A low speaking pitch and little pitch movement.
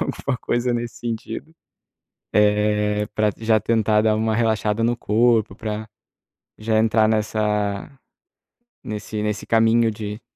Yes: low, 110 Hz; narrow, 1.4 semitones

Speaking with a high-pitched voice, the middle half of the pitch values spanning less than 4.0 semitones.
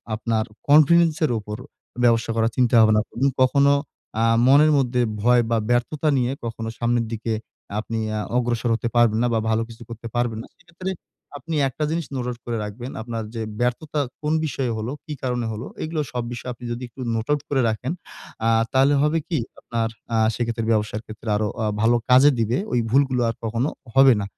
No: low, 120 Hz; average, 3.1 semitones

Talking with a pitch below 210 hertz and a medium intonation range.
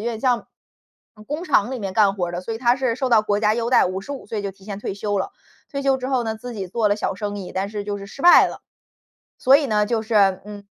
No: high, 215 Hz; average, 3.6 semitones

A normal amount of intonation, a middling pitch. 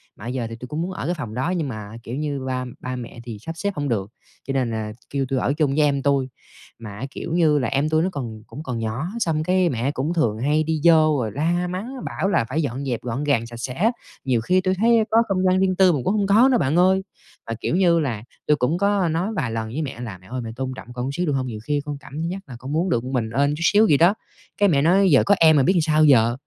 No: wide, 5.9 semitones; medium, 145 Hz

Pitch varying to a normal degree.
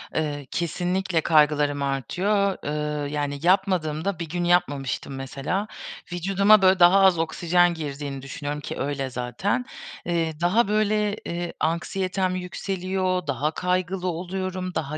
Yes: average, 4.1 semitones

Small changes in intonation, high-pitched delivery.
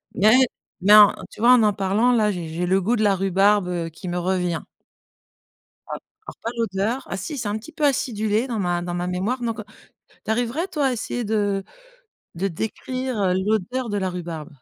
No: average, 4.3 semitones; high, 205 Hz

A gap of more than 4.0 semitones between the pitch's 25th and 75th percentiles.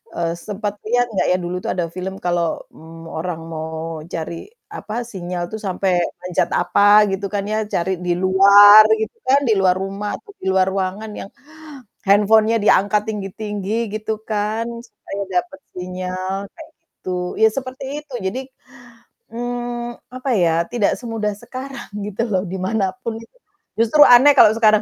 No: average, 3.5 semitones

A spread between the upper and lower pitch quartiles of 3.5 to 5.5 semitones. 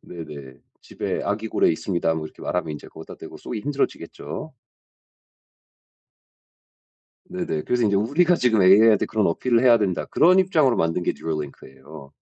No: wide, 7.0 semitones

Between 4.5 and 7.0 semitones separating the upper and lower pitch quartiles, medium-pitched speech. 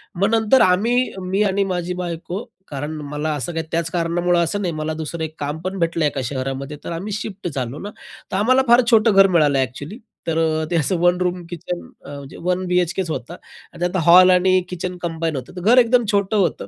No: average, 3.3 semitones; medium, 175 Hz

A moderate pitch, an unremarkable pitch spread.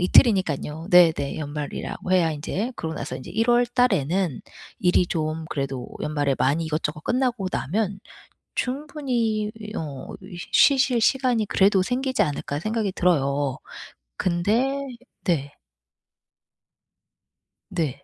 No: medium, 180 Hz; wide, 7.3 semitones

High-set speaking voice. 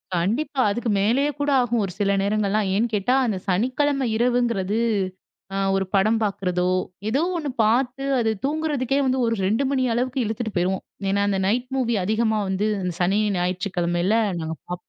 Yes: high, 220 Hz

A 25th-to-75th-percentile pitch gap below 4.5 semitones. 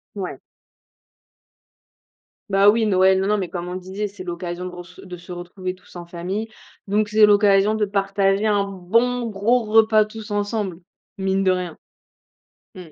Yes: narrow, 2.4 semitones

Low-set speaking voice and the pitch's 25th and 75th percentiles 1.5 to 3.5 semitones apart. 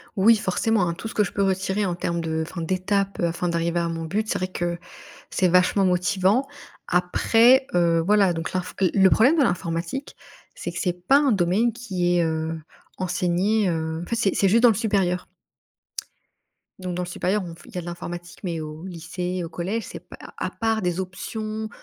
No: medium, 185 Hz; average, 3.1 semitones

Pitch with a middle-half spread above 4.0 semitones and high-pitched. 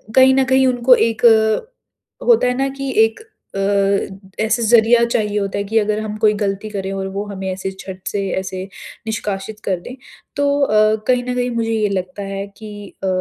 No: average, 3.6 semitones; high, 215 Hz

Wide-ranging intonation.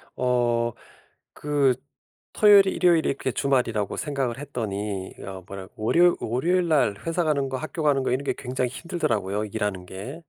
Yes: wide, 6.3 semitones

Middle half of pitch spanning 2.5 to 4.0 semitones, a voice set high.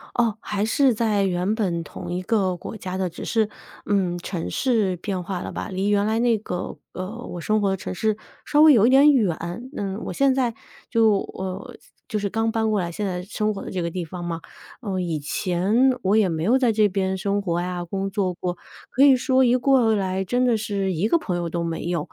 Yes: average, 3.7 semitones; high, 200 Hz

